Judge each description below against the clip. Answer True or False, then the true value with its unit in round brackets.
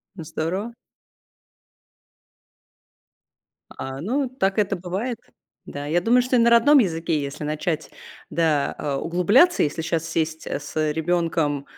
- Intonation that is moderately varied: False (6.3 semitones)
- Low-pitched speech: False (170 Hz)